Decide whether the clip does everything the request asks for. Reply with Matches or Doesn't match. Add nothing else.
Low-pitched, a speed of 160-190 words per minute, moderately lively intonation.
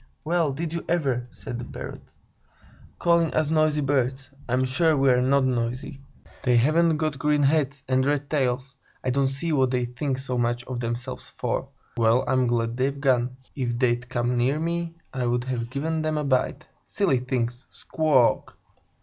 Matches